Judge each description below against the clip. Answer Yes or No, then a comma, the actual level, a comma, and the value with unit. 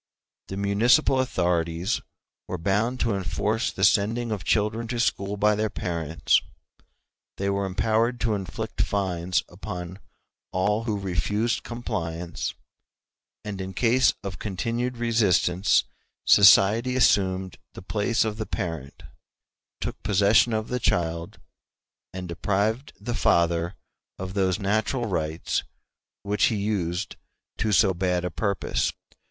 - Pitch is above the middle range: No, low, 100 Hz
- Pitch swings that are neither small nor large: Yes, average, 3.5 semitones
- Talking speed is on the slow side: Yes, slow, 125 wpm